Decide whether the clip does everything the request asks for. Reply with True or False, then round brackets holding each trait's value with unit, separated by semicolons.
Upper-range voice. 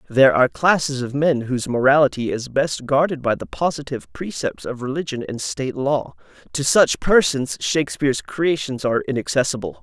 False (135 Hz)